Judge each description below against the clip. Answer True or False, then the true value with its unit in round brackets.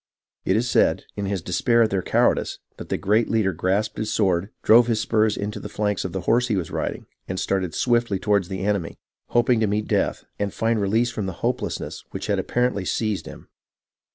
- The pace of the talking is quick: True (210 wpm)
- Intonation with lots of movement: False (2.9 semitones)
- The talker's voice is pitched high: False (105 Hz)